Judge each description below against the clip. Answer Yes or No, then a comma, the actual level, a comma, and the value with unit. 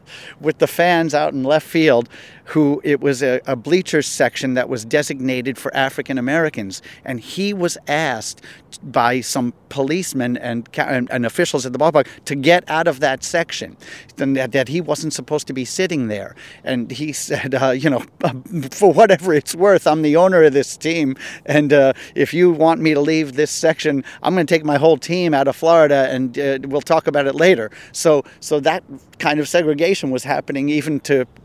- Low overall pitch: No, medium, 150 Hz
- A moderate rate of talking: Yes, average, 195 wpm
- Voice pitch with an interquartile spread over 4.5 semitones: No, average, 3.2 semitones